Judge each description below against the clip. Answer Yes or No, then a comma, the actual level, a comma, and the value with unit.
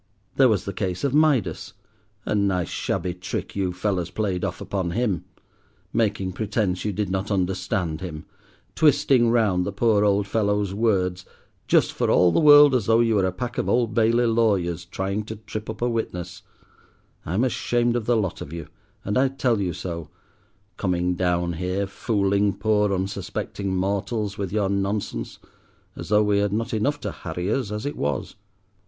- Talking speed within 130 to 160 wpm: No, average, 175 wpm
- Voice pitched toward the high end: No, low, 100 Hz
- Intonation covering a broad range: No, average, 3.4 semitones